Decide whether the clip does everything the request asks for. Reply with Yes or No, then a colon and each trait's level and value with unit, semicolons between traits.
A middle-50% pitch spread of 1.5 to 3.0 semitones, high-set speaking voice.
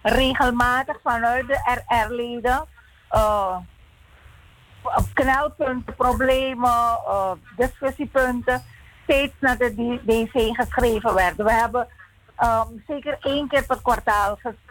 Yes: narrow, 2.5 semitones; high, 245 Hz